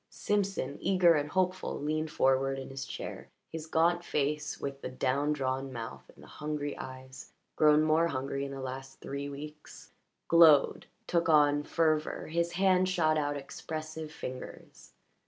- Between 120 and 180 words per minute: Yes, average, 155 wpm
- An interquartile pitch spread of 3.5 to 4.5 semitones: No, average, 2.9 semitones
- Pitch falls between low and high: Yes, medium, 150 Hz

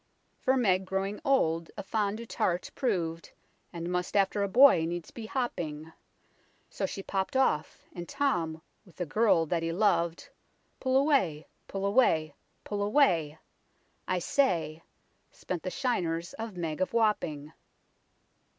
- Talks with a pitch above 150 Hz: Yes, medium, 185 Hz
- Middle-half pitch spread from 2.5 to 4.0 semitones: No, average, 5.1 semitones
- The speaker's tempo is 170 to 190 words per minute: No, average, 140 wpm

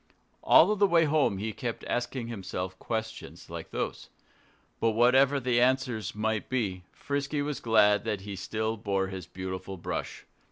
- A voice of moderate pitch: No, low, 110 Hz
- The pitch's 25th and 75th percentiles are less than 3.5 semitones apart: No, average, 4.7 semitones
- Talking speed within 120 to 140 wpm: No, average, 155 wpm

